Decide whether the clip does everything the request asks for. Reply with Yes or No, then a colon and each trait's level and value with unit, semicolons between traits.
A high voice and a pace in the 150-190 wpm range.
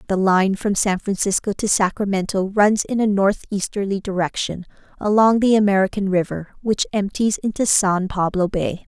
Yes: high, 200 Hz; average, 155 wpm